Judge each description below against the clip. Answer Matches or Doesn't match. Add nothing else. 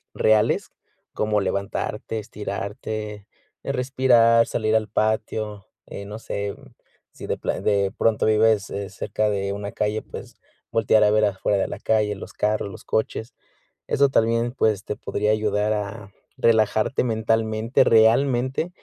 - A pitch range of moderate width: Doesn't match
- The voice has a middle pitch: Doesn't match